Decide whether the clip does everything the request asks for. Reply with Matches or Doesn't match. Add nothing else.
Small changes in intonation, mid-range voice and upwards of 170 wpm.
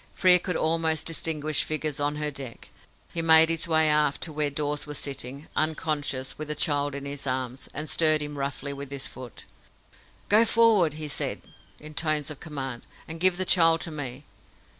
Matches